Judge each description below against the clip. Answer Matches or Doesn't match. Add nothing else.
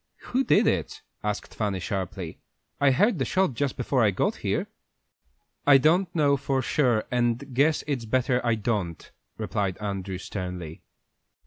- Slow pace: Doesn't match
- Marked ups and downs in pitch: Matches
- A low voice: Matches